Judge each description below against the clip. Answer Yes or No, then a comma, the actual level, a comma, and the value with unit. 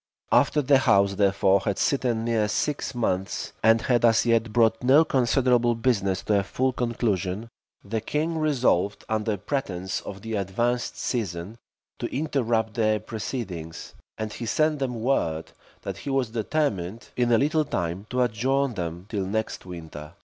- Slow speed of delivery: No, average, 155 wpm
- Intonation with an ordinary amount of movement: Yes, average, 4.3 semitones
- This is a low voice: Yes, low, 115 Hz